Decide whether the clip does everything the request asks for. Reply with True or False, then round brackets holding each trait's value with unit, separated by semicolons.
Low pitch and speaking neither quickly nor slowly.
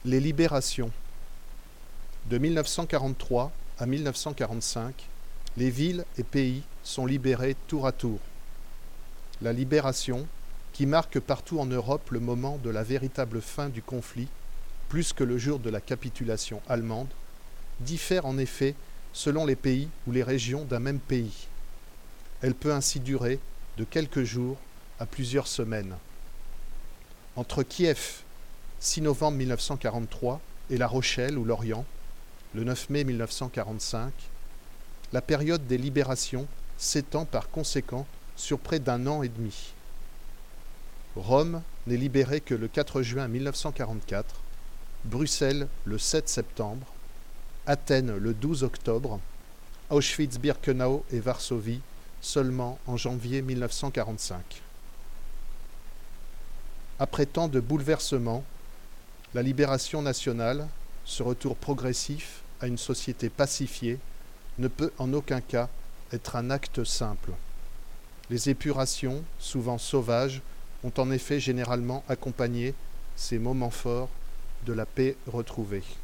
False (125 Hz; 120 wpm)